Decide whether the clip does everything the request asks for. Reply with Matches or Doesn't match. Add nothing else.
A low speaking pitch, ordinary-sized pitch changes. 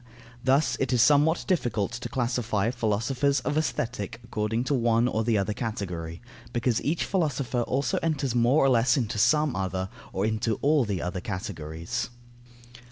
Matches